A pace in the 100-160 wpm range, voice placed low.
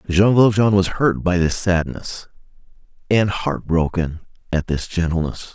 Yes: average, 140 wpm; very low, 90 Hz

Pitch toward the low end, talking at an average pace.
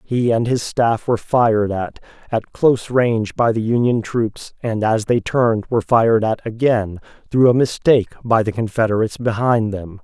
Yes: low, 115 Hz; average, 180 wpm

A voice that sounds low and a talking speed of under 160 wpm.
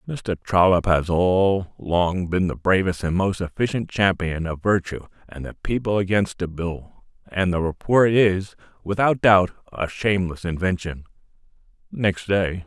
Yes: very low, 95 Hz; average, 145 wpm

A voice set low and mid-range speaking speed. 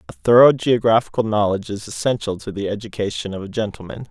Yes: low, 105 Hz; average, 175 wpm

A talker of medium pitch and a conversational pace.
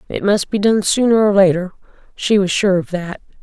No: high, 195 Hz; average, 195 wpm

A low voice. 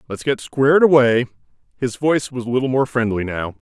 Yes: low, 125 Hz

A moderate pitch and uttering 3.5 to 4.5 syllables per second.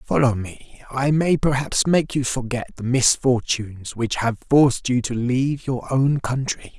No: low, 130 Hz; 4.3 syllables/s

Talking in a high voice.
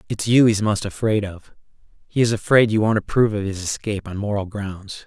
No: low, 105 Hz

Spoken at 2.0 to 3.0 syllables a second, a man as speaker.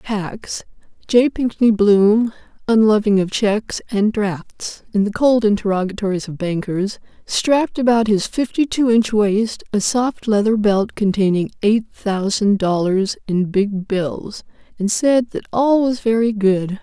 No: 2.8 syllables/s; female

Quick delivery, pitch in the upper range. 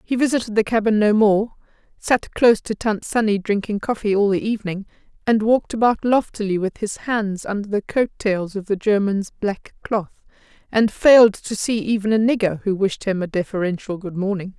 No: average, 190 wpm; high, 210 Hz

